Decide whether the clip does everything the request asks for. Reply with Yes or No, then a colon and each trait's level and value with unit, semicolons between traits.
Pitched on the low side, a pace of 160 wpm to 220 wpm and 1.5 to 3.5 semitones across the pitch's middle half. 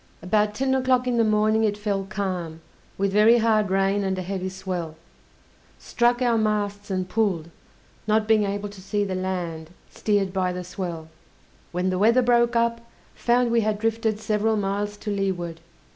No: high, 205 Hz; average, 175 wpm; average, 2.9 semitones